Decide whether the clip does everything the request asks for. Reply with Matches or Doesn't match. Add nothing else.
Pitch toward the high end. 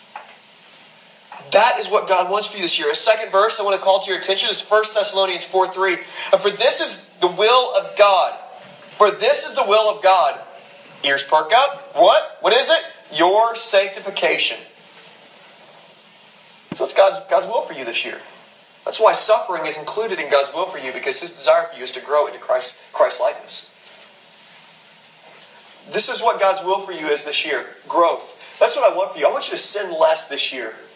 Matches